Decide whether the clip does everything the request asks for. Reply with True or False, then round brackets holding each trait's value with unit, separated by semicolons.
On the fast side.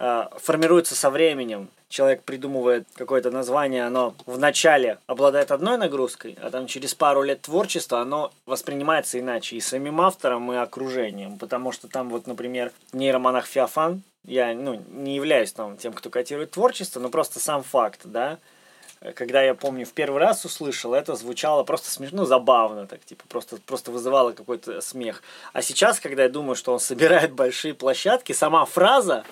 True (165 wpm)